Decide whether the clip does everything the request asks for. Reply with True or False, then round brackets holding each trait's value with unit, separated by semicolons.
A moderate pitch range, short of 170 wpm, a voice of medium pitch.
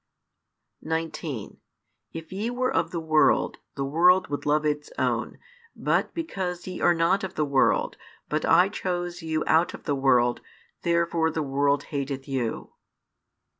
True (3.6 semitones; 150 wpm; 160 Hz)